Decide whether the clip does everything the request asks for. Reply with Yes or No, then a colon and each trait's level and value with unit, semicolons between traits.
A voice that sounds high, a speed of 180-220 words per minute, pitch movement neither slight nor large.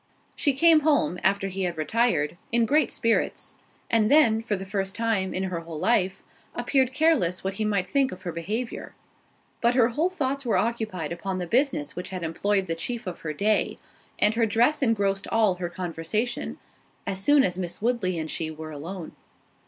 Yes: high, 200 Hz; average, 185 wpm; average, 4.9 semitones